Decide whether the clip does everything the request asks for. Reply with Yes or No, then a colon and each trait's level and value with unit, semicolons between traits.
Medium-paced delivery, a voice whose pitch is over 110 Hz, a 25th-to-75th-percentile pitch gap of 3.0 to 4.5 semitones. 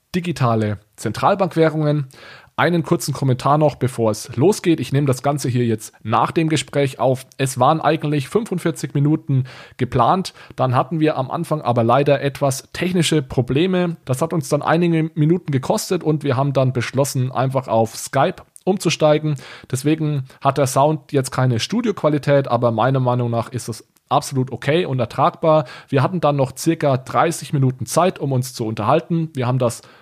Yes: average, 165 wpm; medium, 140 Hz; average, 3.8 semitones